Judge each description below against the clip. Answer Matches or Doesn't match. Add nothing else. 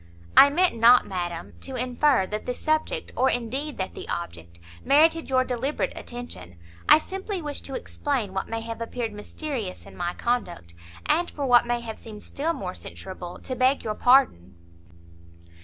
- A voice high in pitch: Matches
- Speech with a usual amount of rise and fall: Doesn't match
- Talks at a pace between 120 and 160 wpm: Doesn't match